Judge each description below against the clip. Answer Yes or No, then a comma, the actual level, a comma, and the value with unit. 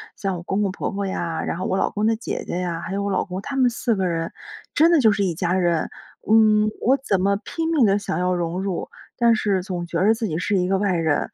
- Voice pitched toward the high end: Yes, high, 195 Hz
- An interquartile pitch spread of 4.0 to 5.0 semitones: No, average, 3.3 semitones